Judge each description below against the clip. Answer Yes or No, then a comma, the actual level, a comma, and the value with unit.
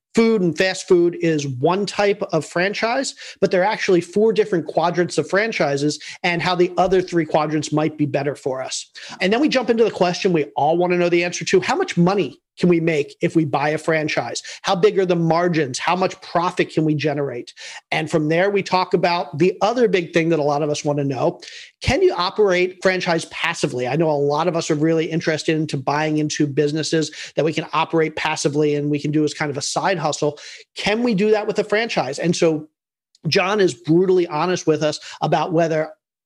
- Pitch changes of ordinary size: Yes, average, 3.4 semitones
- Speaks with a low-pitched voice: No, medium, 170 Hz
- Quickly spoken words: Yes, fast, 220 wpm